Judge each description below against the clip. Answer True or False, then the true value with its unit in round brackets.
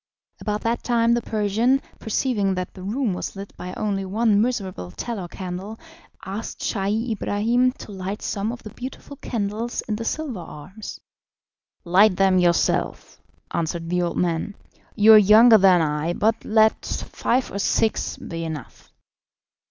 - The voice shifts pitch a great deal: False (3.7 semitones)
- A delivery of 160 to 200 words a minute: False (150 wpm)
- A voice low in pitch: False (205 Hz)